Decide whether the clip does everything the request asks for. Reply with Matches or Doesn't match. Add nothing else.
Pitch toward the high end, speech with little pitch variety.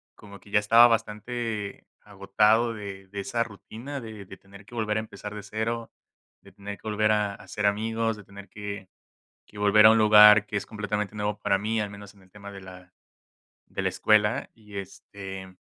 Doesn't match